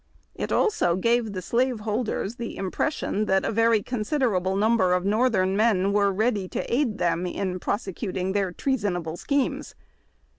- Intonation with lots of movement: No, average, 3.8 semitones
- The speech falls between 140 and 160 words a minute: Yes, average, 155 wpm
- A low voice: No, high, 205 Hz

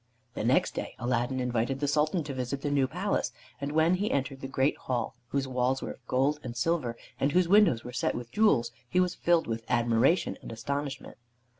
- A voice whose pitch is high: No, low, 135 Hz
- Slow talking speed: No, fast, 205 wpm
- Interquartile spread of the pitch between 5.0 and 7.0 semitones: No, average, 3.8 semitones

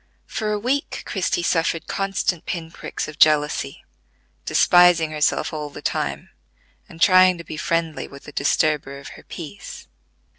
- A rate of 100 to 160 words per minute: Yes, average, 150 wpm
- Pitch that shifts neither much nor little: Yes, average, 3.2 semitones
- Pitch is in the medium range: Yes, medium, 165 Hz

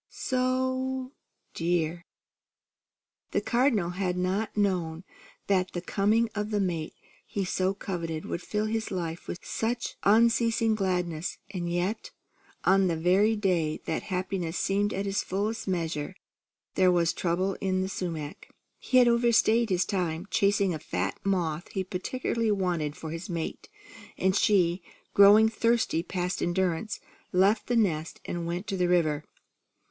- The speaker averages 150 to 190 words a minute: No, average, 140 wpm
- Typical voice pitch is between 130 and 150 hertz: No, medium, 185 Hz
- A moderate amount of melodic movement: Yes, average, 3.5 semitones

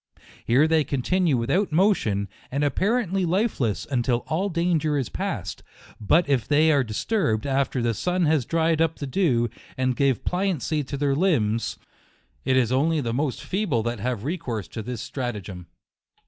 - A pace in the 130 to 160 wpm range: No, average, 175 wpm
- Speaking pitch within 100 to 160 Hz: Yes, medium, 140 Hz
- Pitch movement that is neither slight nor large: No, wide, 5.7 semitones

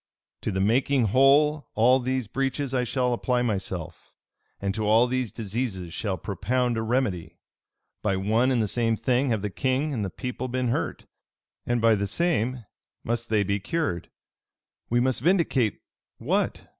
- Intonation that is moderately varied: Yes, average, 3.6 semitones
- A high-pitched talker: No, low, 120 Hz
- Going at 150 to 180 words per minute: Yes, average, 165 wpm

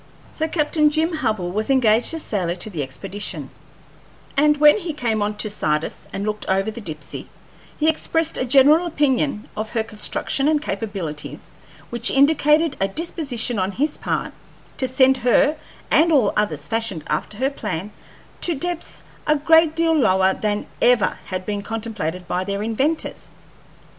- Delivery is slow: No, average, 160 wpm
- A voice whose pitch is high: Yes, high, 230 Hz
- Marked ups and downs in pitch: Yes, wide, 7.0 semitones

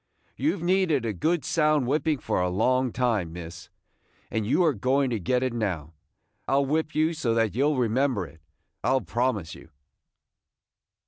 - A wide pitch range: Yes, wide, 6.3 semitones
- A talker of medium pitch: No, low, 125 Hz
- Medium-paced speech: Yes, average, 185 wpm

